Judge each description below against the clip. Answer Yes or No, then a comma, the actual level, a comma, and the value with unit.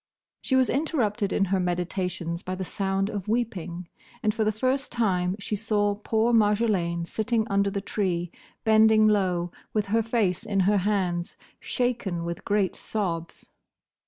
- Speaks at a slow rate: No, average, 155 wpm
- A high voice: Yes, high, 200 Hz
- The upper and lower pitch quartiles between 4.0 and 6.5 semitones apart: No, average, 3.3 semitones